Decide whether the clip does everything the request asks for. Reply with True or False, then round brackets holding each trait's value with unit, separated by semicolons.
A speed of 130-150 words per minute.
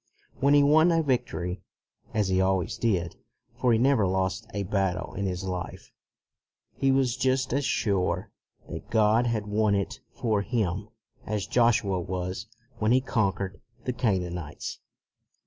True (145 wpm)